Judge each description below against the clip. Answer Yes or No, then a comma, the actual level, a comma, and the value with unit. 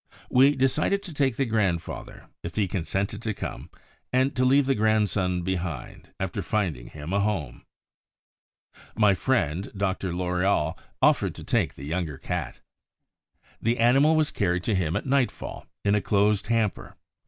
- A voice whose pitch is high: No, low, 100 Hz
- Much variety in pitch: Yes, wide, 5.9 semitones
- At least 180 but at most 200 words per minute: No, average, 155 wpm